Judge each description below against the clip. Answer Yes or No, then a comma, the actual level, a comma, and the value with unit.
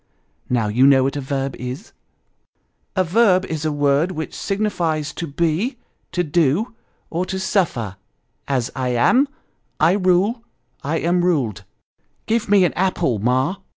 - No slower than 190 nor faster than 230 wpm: No, average, 160 wpm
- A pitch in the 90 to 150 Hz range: No, medium, 160 Hz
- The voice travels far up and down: Yes, wide, 5.8 semitones